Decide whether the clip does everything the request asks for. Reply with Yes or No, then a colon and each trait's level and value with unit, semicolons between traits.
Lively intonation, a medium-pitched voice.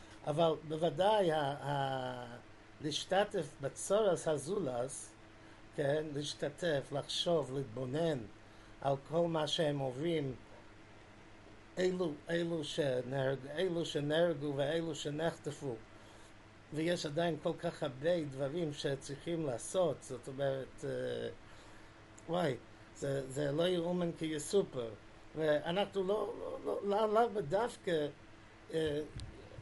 Yes: wide, 6.9 semitones; medium, 145 Hz